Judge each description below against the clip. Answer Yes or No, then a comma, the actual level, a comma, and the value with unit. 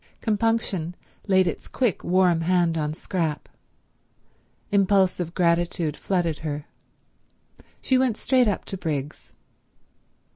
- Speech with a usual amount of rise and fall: Yes, average, 3.4 semitones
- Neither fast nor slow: No, slow, 105 wpm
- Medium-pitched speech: Yes, medium, 180 Hz